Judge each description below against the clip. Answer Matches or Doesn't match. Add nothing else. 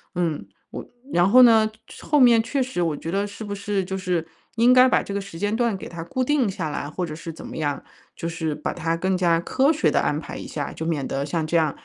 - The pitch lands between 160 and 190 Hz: Matches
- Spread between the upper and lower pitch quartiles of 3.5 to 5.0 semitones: Doesn't match